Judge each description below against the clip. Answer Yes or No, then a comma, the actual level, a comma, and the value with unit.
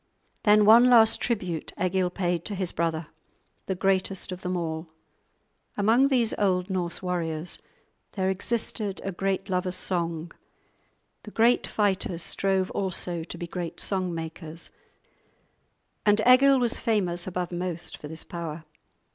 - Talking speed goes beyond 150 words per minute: No, average, 140 wpm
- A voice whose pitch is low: No, medium, 185 Hz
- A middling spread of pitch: Yes, average, 3.1 semitones